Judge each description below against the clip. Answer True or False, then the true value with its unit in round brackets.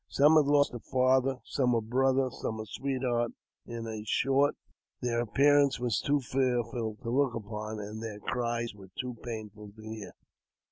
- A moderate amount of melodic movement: True (3.3 semitones)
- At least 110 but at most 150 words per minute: False (160 wpm)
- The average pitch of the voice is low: True (120 Hz)